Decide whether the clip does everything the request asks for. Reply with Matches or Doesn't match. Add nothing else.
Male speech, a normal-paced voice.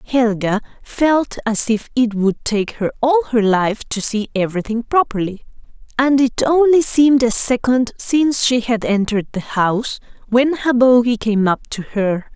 Doesn't match